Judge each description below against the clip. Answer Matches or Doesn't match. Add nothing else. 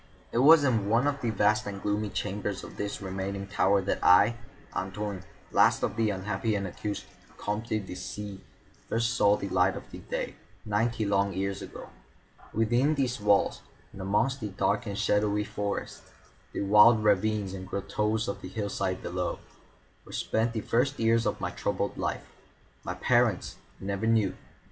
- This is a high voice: Doesn't match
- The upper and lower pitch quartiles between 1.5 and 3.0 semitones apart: Matches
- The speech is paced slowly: Doesn't match